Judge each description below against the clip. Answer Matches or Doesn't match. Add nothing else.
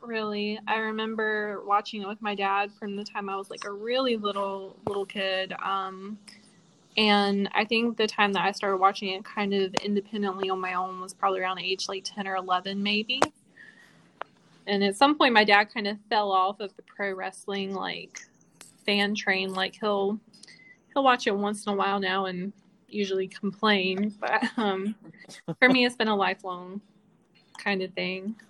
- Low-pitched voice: Doesn't match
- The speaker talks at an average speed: Matches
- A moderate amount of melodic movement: Doesn't match